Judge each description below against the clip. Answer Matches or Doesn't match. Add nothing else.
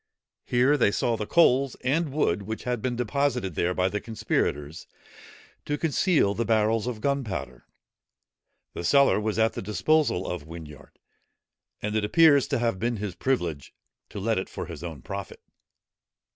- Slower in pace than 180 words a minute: Matches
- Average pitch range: Doesn't match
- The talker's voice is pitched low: Matches